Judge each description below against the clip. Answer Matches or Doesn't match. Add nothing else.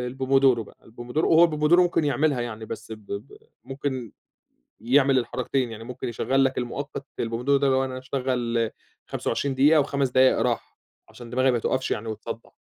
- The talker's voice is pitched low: Matches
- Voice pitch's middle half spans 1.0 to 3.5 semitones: Matches